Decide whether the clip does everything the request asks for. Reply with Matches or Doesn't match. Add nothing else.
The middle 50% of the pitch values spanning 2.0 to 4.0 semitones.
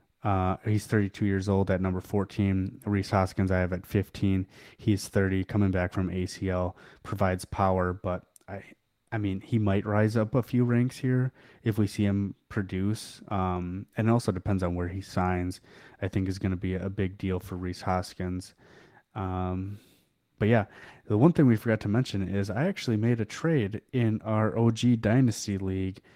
Matches